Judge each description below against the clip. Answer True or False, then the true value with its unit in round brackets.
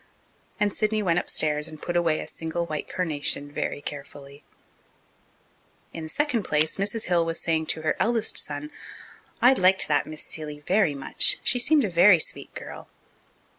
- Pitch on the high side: False (165 Hz)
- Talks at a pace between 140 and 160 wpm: False (170 wpm)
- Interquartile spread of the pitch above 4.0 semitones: True (5.0 semitones)